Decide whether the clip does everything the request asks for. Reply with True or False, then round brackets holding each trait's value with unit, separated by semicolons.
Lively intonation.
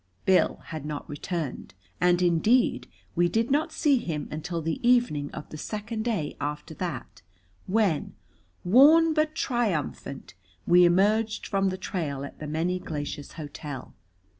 True (6.8 semitones)